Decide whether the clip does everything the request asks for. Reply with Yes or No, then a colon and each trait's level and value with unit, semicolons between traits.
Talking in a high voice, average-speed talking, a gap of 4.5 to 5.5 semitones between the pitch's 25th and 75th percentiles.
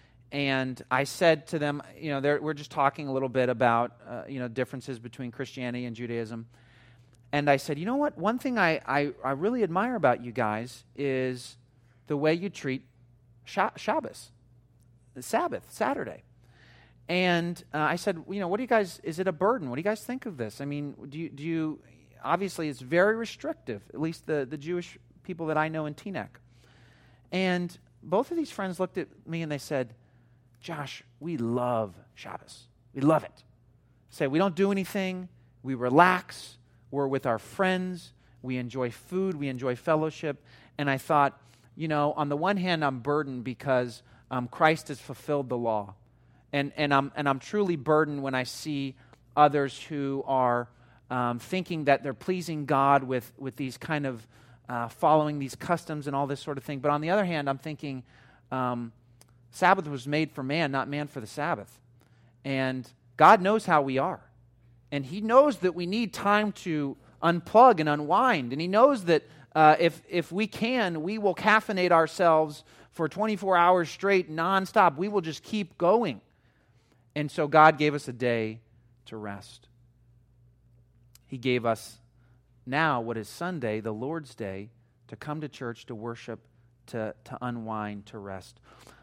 No: medium, 140 Hz; average, 180 wpm; average, 5.1 semitones